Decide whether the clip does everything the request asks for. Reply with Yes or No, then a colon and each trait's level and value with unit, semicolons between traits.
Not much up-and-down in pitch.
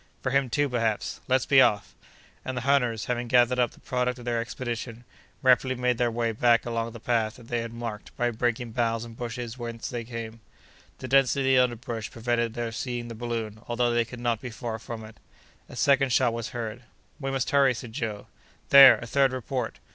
Yes: narrow, 1.5 semitones